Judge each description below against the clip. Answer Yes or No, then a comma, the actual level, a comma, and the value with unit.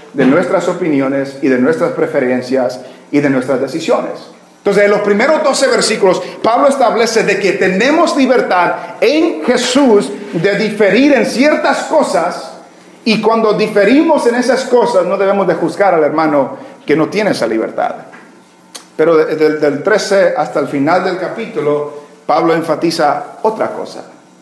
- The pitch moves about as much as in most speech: No, wide, 7.6 semitones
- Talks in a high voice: Yes, high, 200 Hz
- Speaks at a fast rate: No, average, 145 wpm